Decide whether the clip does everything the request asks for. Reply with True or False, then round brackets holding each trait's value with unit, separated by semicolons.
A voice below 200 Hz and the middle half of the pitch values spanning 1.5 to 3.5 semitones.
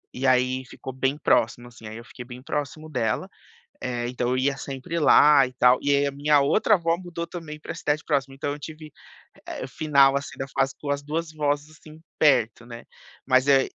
True (140 Hz; 3.0 semitones)